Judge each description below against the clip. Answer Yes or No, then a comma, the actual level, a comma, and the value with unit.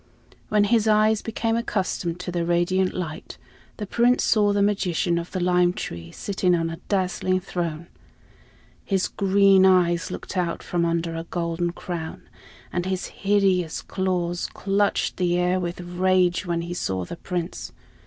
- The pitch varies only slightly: Yes, narrow, 2.2 semitones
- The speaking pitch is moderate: Yes, medium, 180 Hz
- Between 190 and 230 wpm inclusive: No, average, 155 wpm